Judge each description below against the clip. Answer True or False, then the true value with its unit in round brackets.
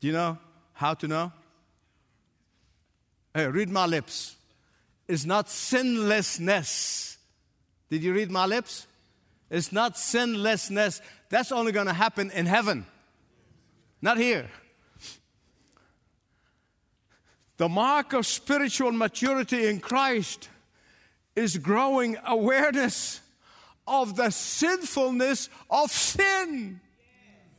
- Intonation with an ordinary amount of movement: False (5.9 semitones)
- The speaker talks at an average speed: False (100 wpm)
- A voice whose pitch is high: True (215 Hz)